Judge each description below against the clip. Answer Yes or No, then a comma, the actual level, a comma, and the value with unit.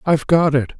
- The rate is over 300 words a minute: No, fast, 225 wpm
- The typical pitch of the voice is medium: Yes, medium, 150 Hz